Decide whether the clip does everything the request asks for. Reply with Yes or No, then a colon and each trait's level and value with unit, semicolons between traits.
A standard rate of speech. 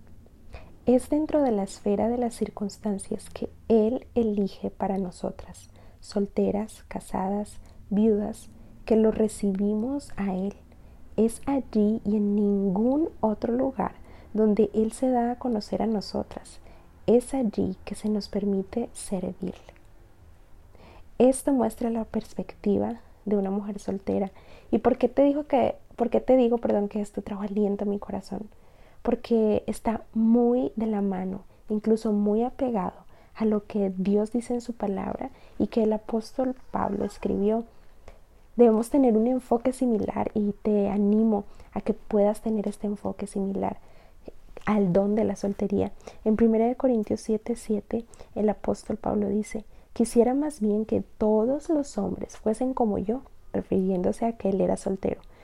Yes: average, 150 wpm